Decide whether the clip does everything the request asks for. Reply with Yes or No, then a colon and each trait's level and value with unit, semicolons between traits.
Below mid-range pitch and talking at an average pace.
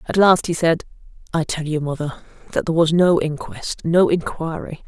No: medium, 160 Hz; average, 170 wpm